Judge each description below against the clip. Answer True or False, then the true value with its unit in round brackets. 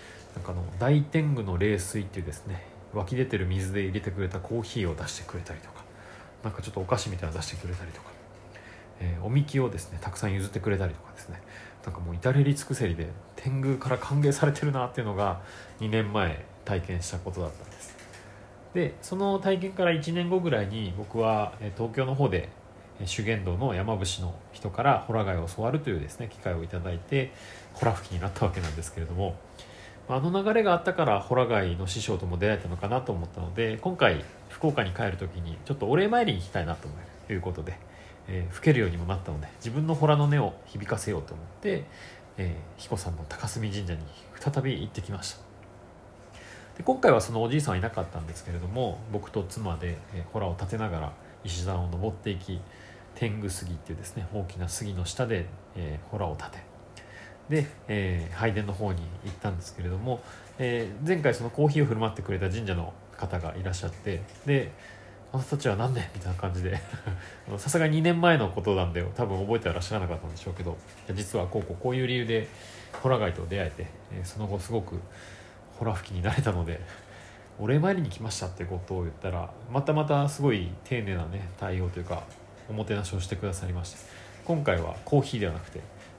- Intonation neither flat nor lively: True (4.3 semitones)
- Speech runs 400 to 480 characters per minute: True (405 characters per minute)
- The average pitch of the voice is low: True (100 Hz)